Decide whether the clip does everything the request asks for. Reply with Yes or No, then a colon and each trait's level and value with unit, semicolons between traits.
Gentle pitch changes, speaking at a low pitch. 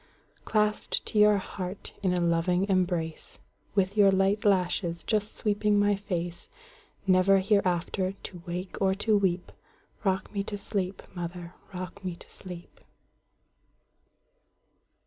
No: narrow, 2.3 semitones; high, 190 Hz